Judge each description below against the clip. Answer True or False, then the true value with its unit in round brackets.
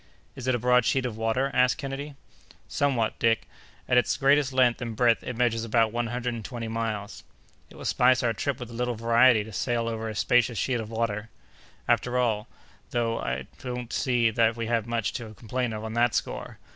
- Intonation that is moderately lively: False (1.8 semitones)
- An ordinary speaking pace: False (210 wpm)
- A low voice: True (120 Hz)